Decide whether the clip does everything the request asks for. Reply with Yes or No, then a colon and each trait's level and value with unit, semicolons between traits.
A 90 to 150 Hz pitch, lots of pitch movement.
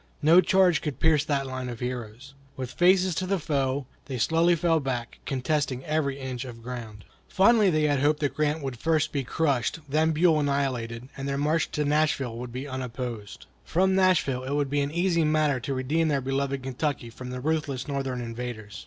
No: medium, 140 Hz; average, 3.6 semitones